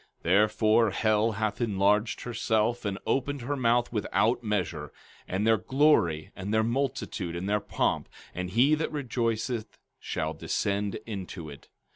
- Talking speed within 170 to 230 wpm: No, average, 145 wpm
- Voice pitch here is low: Yes, low, 110 Hz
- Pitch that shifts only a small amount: No, average, 3.3 semitones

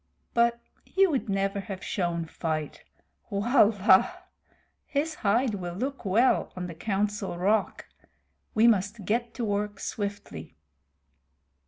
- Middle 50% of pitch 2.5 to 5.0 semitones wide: Yes, average, 4.1 semitones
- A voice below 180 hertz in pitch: No, high, 205 Hz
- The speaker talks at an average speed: No, slow, 115 wpm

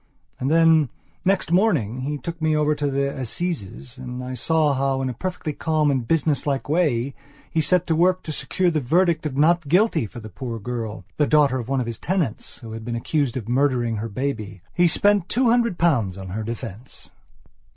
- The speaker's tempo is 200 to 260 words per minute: Yes, fast, 205 wpm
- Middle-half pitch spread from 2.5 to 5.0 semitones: No, wide, 5.4 semitones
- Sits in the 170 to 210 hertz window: No, medium, 140 Hz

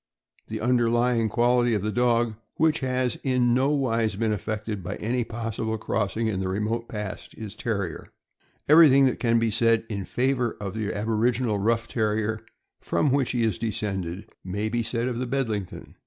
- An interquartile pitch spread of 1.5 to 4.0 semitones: Yes, narrow, 2.5 semitones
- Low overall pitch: Yes, low, 115 Hz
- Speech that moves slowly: No, average, 170 wpm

